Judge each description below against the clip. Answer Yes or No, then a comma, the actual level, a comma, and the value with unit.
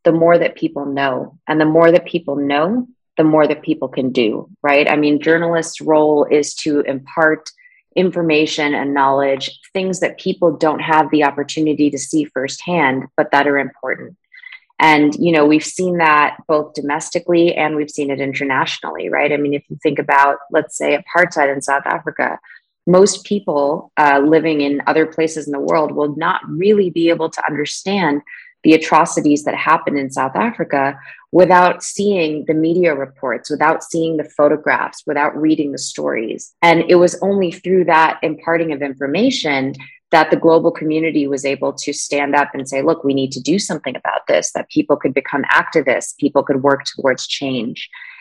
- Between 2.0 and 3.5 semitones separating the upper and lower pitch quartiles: Yes, average, 2.8 semitones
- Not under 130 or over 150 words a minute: No, average, 180 wpm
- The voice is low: No, medium, 155 Hz